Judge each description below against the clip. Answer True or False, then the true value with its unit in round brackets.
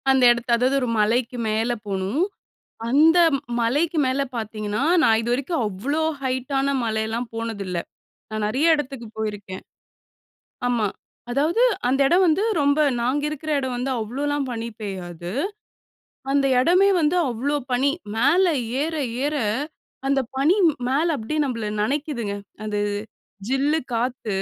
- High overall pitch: True (255 Hz)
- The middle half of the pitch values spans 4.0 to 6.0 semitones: True (4.5 semitones)